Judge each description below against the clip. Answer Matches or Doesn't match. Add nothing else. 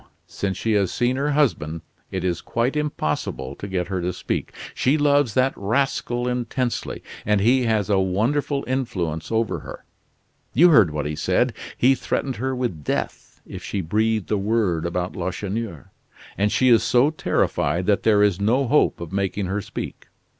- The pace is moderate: Matches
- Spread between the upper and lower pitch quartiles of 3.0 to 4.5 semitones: Doesn't match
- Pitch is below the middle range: Matches